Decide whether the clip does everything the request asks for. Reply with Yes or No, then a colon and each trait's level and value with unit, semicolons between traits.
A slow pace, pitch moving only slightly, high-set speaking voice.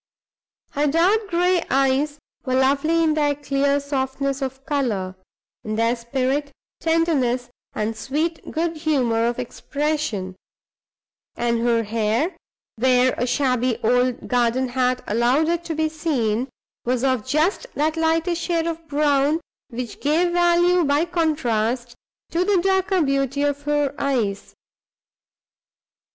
No: slow, 130 wpm; average, 4.5 semitones; very high, 280 Hz